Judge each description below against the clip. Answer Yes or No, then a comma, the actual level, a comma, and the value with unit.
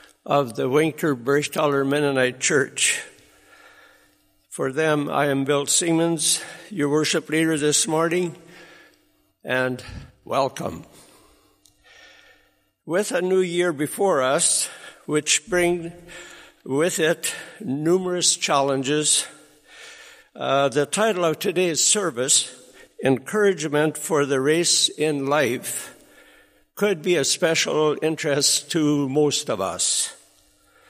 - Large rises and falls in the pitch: No, average, 3.6 semitones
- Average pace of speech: No, slow, 100 wpm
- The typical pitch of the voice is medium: Yes, medium, 155 Hz